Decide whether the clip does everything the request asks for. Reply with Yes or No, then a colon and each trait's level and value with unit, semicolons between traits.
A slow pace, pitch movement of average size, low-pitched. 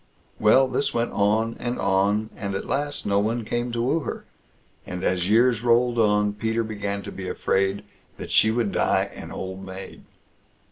No: average, 180 wpm; average, 3.1 semitones; low, 110 Hz